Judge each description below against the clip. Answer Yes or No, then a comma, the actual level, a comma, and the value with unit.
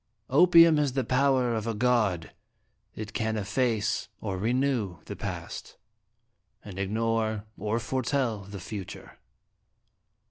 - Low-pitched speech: Yes, low, 115 Hz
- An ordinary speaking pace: No, slow, 120 wpm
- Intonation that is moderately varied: Yes, average, 3.6 semitones